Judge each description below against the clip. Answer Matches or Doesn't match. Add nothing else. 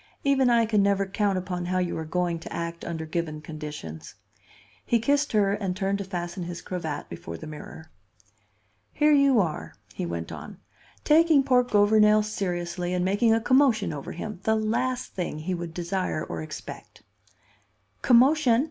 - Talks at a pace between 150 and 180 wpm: Matches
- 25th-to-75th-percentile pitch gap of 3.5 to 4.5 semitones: Doesn't match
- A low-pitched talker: Doesn't match